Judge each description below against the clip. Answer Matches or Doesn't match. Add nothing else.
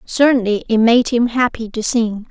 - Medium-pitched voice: Doesn't match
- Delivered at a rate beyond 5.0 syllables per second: Doesn't match